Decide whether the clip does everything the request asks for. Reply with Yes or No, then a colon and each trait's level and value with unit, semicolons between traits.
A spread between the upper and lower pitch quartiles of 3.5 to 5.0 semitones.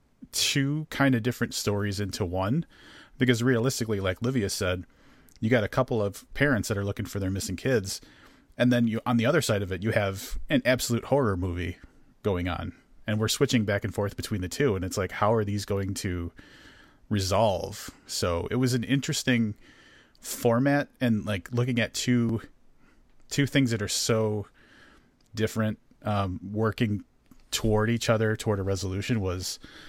Yes: average, 3.8 semitones